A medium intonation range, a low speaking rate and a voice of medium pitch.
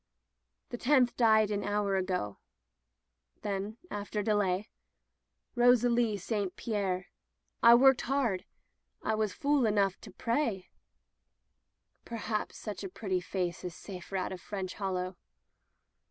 No: average, 3.6 semitones; slow, 125 wpm; high, 205 Hz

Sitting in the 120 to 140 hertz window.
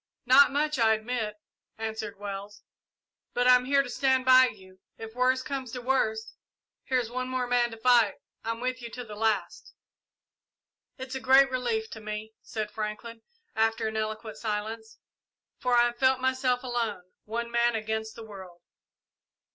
No: high, 235 Hz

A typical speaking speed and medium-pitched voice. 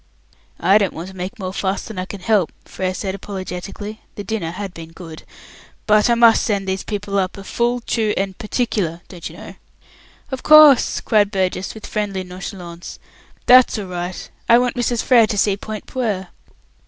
No: average, 185 wpm; high, 200 Hz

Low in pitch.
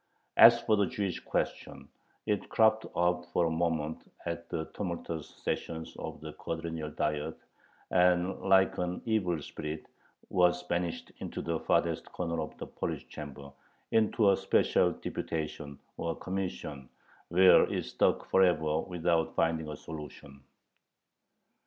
Yes: very low, 85 Hz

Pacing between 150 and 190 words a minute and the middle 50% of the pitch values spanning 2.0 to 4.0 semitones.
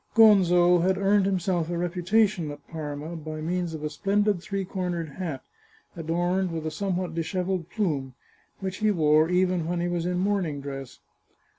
Yes: average, 165 wpm; average, 3.0 semitones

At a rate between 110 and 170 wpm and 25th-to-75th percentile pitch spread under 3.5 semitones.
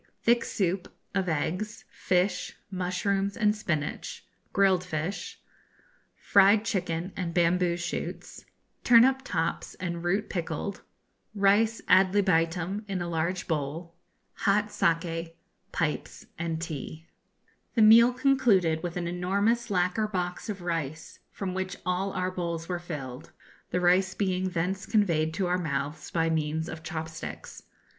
Yes: slow, 135 wpm; average, 3.1 semitones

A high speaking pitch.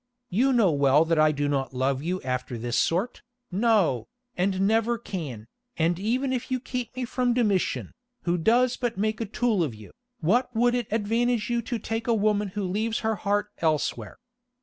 Yes: high, 210 Hz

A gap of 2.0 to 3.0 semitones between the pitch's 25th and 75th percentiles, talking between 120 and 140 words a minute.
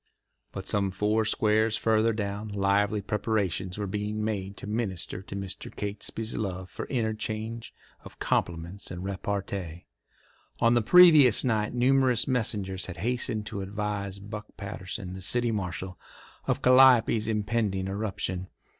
Yes: narrow, 2.4 semitones; slow, 135 wpm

